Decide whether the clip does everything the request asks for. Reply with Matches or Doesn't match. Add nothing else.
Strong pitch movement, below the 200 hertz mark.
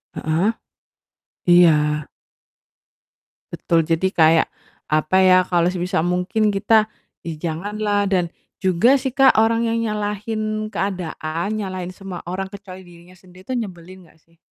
Doesn't match